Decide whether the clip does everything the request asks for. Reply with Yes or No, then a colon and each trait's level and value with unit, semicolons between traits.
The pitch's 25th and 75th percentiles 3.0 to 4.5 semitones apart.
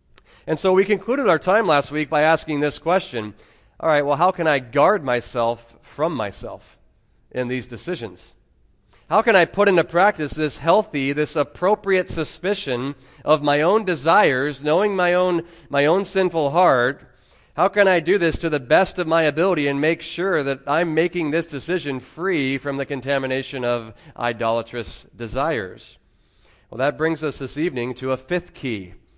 No: average, 5.1 semitones